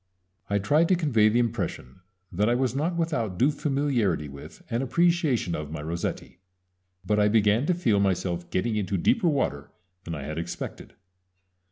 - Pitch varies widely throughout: Yes, wide, 8.2 semitones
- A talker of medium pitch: No, low, 110 Hz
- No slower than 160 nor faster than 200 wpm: Yes, average, 170 wpm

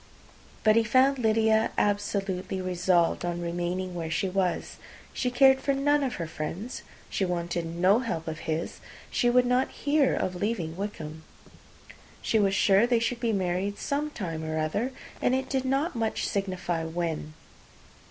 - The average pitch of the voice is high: Yes, high, 195 Hz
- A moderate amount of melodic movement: No, wide, 6.0 semitones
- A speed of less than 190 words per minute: Yes, average, 160 wpm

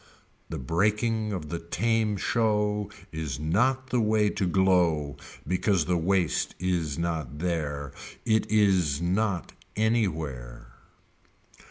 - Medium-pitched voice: No, very low, 90 Hz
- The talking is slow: Yes, slow, 120 wpm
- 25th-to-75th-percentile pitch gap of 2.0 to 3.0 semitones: No, average, 5.1 semitones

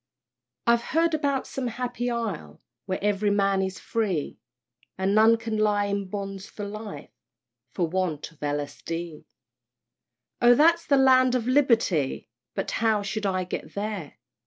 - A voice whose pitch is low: No, high, 205 Hz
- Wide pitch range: No, average, 4.2 semitones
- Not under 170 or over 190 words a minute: No, average, 155 wpm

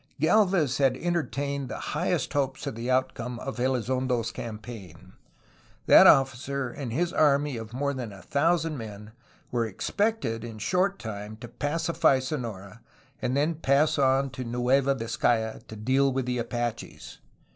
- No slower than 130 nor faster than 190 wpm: Yes, average, 155 wpm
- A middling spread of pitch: Yes, average, 3.5 semitones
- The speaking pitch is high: No, low, 130 Hz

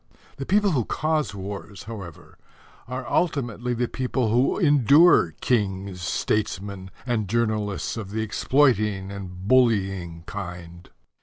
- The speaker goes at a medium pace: No, slow, 120 wpm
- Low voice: Yes, low, 105 Hz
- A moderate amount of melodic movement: Yes, average, 4.7 semitones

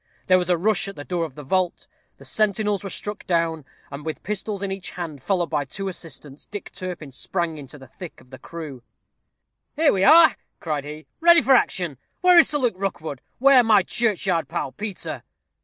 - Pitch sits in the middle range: Yes, medium, 180 Hz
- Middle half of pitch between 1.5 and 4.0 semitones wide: No, average, 5.1 semitones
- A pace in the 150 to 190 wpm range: No, fast, 205 wpm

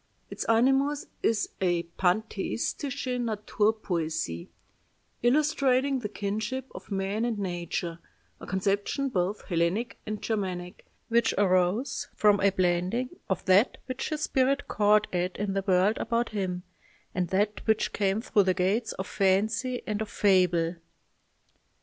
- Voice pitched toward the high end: Yes, high, 205 Hz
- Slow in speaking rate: Yes, slow, 130 wpm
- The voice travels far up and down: No, average, 4.1 semitones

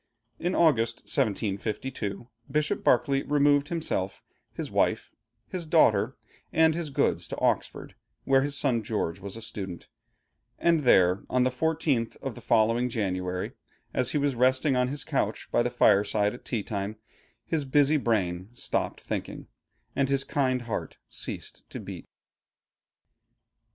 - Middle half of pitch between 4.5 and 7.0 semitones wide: Yes, average, 5.3 semitones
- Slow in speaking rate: No, average, 145 wpm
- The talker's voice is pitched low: Yes, low, 125 Hz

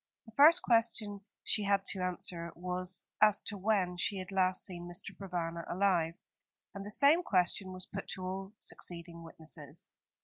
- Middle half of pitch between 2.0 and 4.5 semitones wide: Yes, narrow, 2.5 semitones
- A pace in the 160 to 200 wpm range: Yes, average, 165 wpm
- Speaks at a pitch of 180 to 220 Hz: Yes, medium, 185 Hz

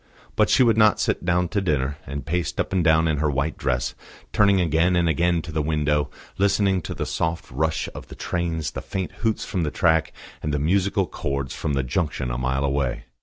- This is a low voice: Yes, very low, 80 Hz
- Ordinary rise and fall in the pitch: Yes, average, 3.8 semitones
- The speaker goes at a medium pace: No, fast, 220 wpm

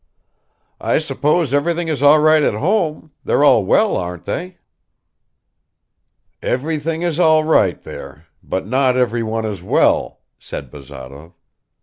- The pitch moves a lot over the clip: Yes, wide, 9.0 semitones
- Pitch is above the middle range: No, medium, 140 Hz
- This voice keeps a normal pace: No, slow, 125 wpm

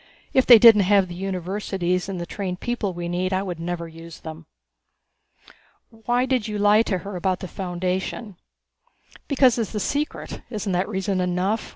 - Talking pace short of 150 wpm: No, average, 175 wpm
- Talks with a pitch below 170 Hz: No, high, 190 Hz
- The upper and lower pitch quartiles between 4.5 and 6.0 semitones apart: No, average, 3.1 semitones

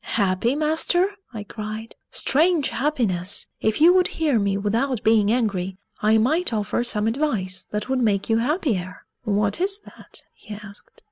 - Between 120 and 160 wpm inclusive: Yes, average, 155 wpm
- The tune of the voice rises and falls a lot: Yes, wide, 6.0 semitones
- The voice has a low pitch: No, high, 225 Hz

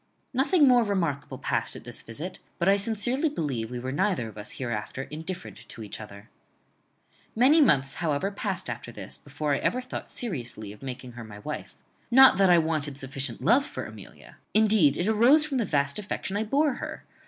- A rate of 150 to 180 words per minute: No, average, 190 wpm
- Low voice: No, medium, 165 Hz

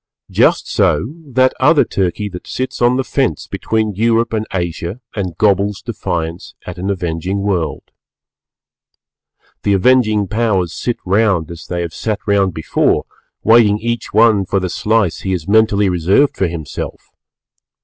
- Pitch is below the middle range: Yes, low, 100 Hz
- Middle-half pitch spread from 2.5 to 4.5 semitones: Yes, average, 4.0 semitones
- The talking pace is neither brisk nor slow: Yes, average, 150 wpm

